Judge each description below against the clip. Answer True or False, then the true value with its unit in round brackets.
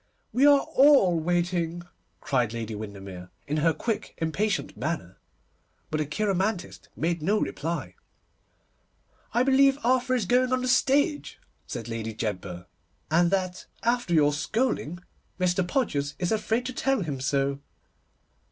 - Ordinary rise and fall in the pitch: False (8.9 semitones)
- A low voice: False (175 Hz)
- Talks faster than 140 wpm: False (135 wpm)